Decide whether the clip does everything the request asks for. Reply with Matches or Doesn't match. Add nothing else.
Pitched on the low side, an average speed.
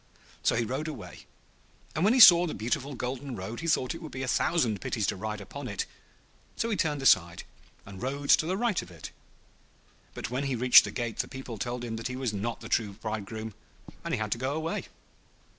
Doesn't match